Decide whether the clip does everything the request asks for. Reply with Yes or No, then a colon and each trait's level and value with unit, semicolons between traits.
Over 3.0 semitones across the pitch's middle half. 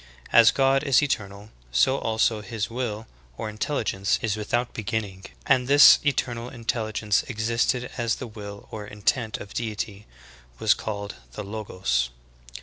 No: average, 2.7 semitones